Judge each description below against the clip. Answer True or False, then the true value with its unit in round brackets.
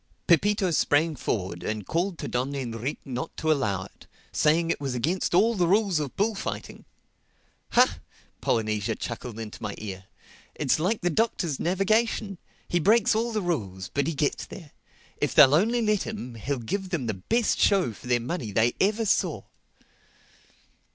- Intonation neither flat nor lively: False (8.5 semitones)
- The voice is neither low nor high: True (155 Hz)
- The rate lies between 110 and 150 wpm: False (165 wpm)